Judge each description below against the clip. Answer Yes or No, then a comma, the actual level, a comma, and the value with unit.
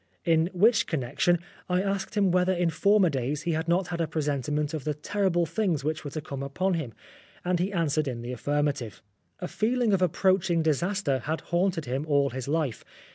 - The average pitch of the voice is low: No, medium, 165 Hz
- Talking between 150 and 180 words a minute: No, average, 200 wpm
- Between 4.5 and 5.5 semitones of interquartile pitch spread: No, average, 4.0 semitones